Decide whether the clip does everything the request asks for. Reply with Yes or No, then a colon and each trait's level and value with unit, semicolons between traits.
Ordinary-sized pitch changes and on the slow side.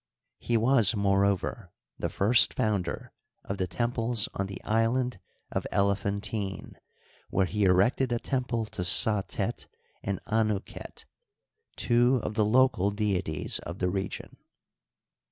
Yes: average, 3.2 semitones; slow, 125 wpm